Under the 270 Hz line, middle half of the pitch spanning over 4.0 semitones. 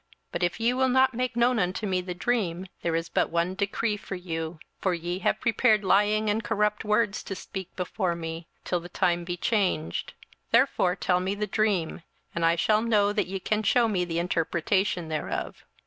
No: high, 190 Hz; average, 3.6 semitones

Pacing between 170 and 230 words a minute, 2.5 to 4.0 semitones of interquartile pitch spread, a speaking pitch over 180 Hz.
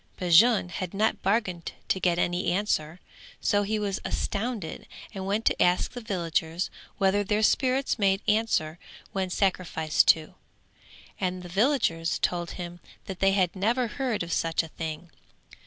No: average, 155 wpm; average, 3.4 semitones; high, 190 Hz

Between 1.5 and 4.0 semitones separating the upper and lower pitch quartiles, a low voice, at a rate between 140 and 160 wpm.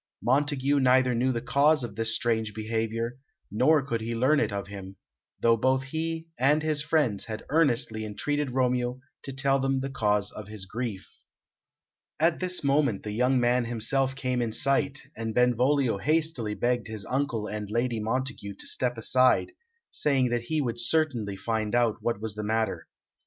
No: average, 3.6 semitones; low, 125 Hz; average, 175 wpm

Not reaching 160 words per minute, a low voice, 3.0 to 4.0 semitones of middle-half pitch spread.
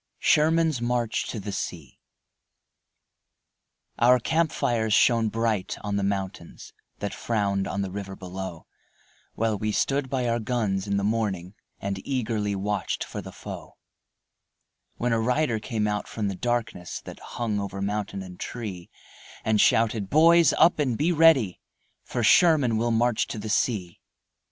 Yes: average, 150 wpm; low, 110 Hz; average, 3.5 semitones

